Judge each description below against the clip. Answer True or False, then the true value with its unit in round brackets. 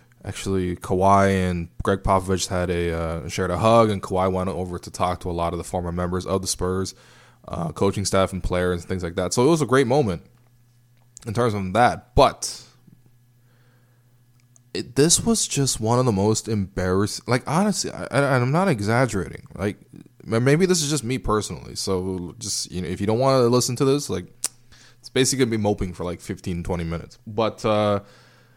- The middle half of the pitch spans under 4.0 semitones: False (4.8 semitones)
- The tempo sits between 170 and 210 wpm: True (200 wpm)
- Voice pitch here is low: True (105 Hz)